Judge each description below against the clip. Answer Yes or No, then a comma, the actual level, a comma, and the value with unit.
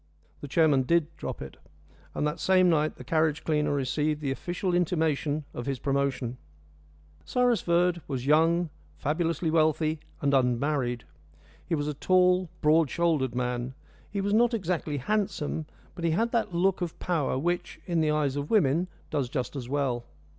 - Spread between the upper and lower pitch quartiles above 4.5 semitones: No, average, 4.0 semitones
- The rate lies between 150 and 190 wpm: Yes, average, 165 wpm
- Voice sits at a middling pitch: Yes, medium, 155 Hz